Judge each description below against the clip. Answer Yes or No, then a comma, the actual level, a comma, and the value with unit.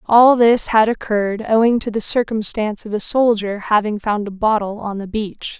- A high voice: Yes, high, 215 Hz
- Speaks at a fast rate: No, average, 195 wpm